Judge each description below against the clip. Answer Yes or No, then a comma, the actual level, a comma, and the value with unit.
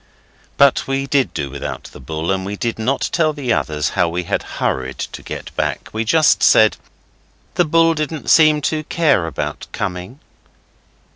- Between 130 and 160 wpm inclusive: No, average, 170 wpm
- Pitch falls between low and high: No, low, 120 Hz